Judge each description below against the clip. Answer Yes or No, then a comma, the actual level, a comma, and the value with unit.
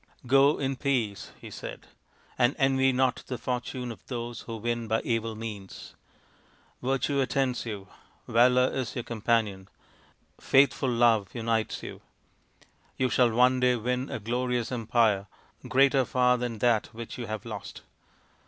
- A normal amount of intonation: No, narrow, 2.2 semitones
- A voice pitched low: Yes, low, 120 Hz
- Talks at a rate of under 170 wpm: Yes, average, 150 wpm